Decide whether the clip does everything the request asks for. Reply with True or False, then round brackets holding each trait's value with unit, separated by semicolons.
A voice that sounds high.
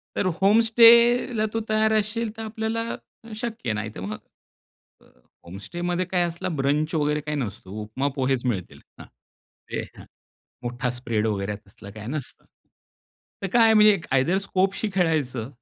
False (165 Hz)